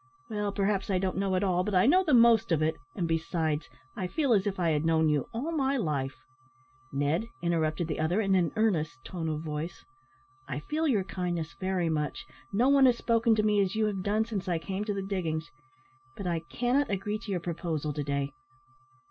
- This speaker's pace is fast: Yes, fast, 215 wpm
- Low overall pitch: No, medium, 185 Hz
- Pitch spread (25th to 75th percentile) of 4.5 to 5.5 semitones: Yes, average, 5.1 semitones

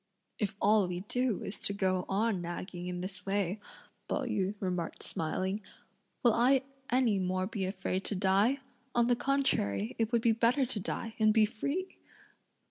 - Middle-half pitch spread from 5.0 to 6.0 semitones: No, average, 3.9 semitones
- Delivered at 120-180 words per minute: Yes, average, 170 wpm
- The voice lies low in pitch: No, high, 205 Hz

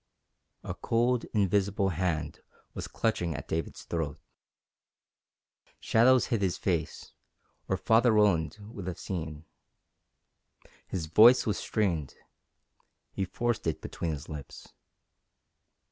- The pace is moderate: No, slow, 110 wpm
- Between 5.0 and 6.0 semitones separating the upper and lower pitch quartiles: Yes, wide, 5.4 semitones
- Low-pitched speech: Yes, very low, 95 Hz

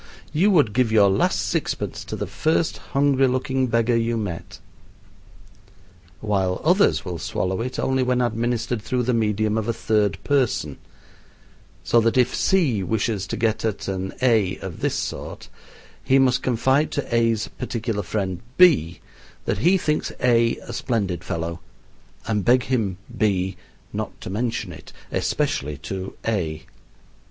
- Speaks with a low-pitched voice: Yes, low, 115 Hz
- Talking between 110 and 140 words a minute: No, average, 150 wpm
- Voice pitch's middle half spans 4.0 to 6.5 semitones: Yes, average, 4.5 semitones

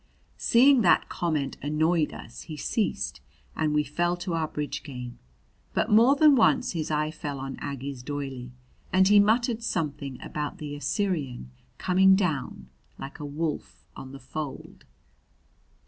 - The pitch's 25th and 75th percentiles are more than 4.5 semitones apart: Yes, average, 5.1 semitones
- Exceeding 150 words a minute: No, average, 145 wpm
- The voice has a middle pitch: Yes, medium, 150 Hz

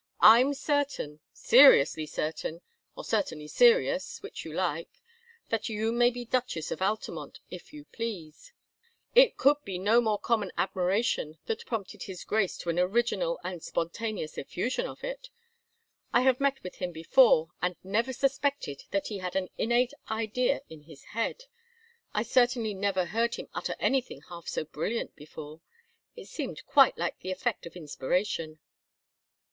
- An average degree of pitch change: No, wide, 6.4 semitones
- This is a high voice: Yes, high, 215 Hz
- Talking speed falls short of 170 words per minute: Yes, average, 150 wpm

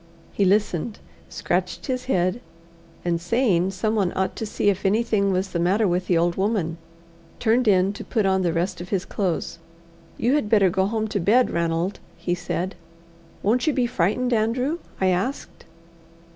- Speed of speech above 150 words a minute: Yes, average, 170 wpm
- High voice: Yes, high, 195 Hz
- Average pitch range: Yes, average, 3.9 semitones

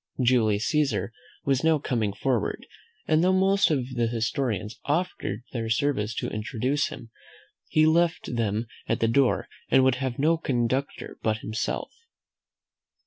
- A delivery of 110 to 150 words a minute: Yes, average, 140 wpm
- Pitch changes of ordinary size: Yes, average, 4.4 semitones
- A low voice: Yes, low, 125 Hz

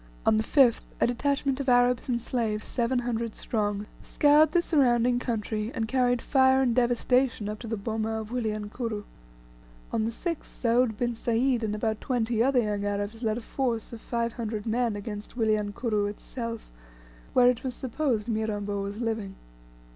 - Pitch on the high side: Yes, high, 230 Hz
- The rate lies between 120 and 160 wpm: No, average, 170 wpm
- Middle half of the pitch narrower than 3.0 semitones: Yes, narrow, 2.5 semitones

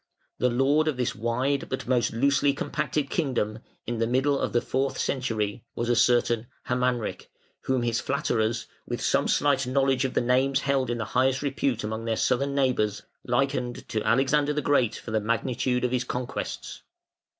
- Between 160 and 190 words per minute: Yes, average, 175 wpm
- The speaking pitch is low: Yes, low, 125 Hz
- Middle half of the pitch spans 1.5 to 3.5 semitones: Yes, narrow, 2.6 semitones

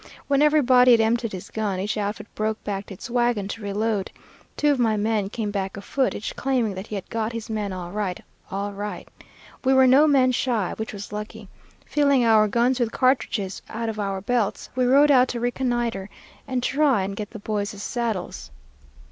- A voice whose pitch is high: Yes, high, 220 Hz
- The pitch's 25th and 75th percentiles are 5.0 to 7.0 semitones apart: No, average, 3.6 semitones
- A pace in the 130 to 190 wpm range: No, average, 200 wpm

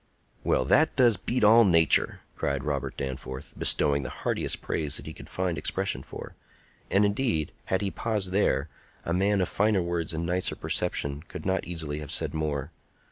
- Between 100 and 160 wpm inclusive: No, average, 180 wpm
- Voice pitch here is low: Yes, very low, 85 Hz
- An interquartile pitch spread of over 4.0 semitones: Yes, wide, 5.6 semitones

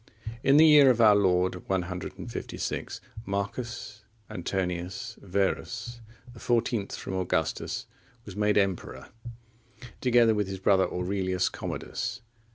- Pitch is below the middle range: Yes, low, 100 Hz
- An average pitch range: Yes, average, 4.1 semitones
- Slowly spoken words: Yes, slow, 110 wpm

